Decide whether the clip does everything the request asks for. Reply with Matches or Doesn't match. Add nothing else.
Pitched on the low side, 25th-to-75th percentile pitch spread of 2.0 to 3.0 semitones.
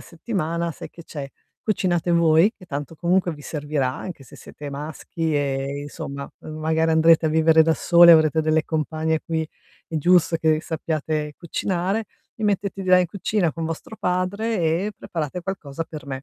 Doesn't match